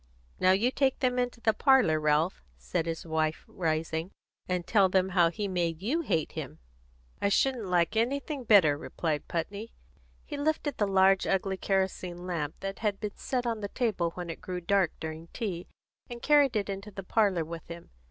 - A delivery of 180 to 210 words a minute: Yes, average, 185 wpm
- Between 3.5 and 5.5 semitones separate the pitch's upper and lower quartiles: Yes, average, 5.0 semitones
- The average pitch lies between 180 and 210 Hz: Yes, high, 190 Hz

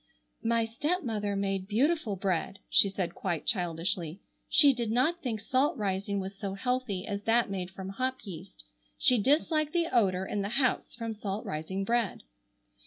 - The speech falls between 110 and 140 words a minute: No, average, 165 wpm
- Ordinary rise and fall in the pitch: Yes, average, 4.5 semitones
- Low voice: No, high, 205 Hz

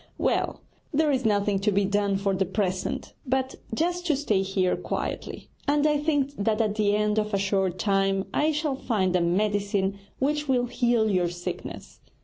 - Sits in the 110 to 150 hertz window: No, high, 210 Hz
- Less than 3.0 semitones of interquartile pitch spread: No, average, 5.3 semitones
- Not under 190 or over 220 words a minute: No, average, 180 wpm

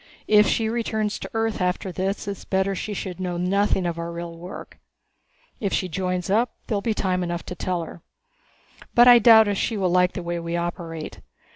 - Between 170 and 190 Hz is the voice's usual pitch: Yes, medium, 185 Hz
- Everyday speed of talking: No, fast, 210 wpm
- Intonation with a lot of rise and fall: No, average, 3.3 semitones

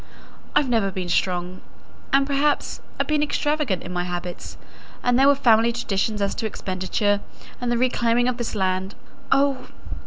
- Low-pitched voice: No, high, 230 Hz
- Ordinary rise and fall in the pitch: No, wide, 6.1 semitones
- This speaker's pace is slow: No, average, 160 wpm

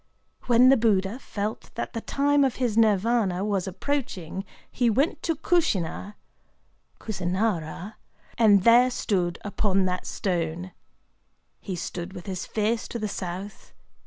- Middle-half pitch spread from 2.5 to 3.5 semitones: No, average, 4.2 semitones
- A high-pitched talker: Yes, high, 205 Hz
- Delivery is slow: Yes, slow, 130 wpm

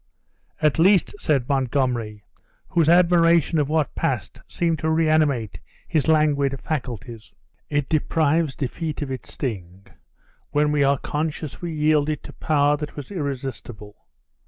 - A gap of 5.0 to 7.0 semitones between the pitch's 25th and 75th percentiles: No, average, 3.1 semitones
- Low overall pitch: No, medium, 145 Hz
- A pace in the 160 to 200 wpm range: No, slow, 135 wpm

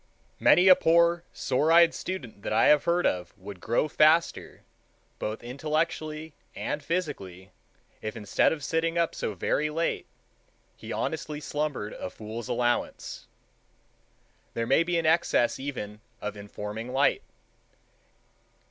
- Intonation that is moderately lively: No, wide, 7.1 semitones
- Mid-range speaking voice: Yes, medium, 145 Hz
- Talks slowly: Yes, slow, 130 wpm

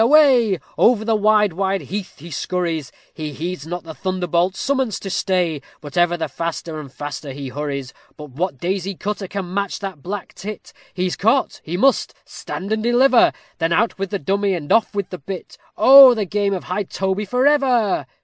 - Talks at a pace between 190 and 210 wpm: Yes, average, 195 wpm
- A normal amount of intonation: Yes, average, 4.1 semitones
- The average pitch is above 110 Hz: Yes, high, 190 Hz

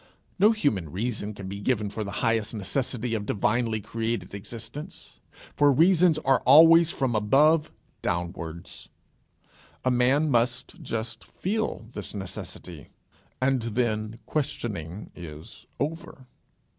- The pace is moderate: No, slow, 120 wpm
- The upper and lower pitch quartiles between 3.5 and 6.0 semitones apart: Yes, average, 5.1 semitones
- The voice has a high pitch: No, low, 115 Hz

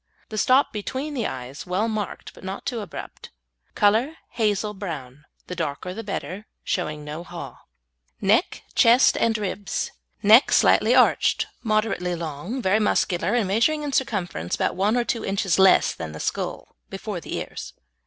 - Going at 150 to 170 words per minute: Yes, average, 160 wpm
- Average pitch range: Yes, average, 4.2 semitones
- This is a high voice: Yes, high, 205 Hz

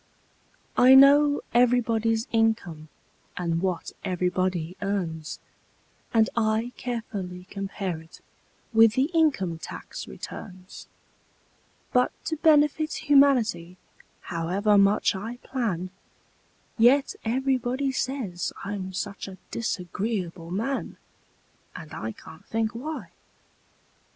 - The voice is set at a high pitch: Yes, high, 220 Hz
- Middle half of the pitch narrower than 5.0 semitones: No, wide, 5.5 semitones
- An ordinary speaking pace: No, slow, 95 wpm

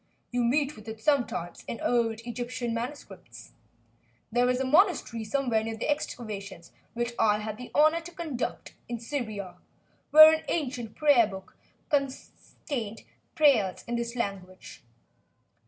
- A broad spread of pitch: No, average, 4.3 semitones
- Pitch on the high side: Yes, high, 240 Hz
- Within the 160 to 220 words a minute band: No, average, 140 wpm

